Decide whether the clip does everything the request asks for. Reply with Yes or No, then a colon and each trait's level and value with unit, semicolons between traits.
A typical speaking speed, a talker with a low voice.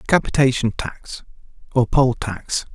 No: slow, 130 wpm; low, 125 Hz